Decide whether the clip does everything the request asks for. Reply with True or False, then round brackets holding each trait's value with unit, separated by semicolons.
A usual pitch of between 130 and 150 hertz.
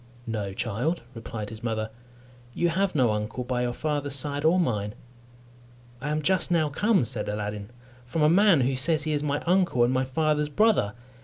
True (140 Hz)